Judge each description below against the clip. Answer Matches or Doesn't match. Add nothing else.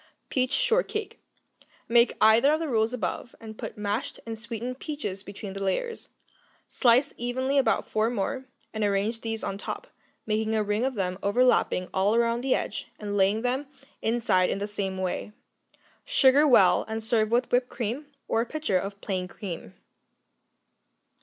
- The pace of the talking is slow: Doesn't match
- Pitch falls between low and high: Doesn't match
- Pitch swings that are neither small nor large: Matches